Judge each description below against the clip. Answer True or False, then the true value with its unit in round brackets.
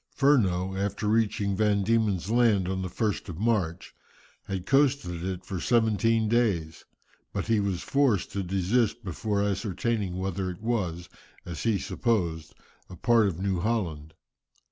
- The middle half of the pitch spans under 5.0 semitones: True (3.8 semitones)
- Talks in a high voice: False (100 Hz)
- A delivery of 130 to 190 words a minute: True (145 wpm)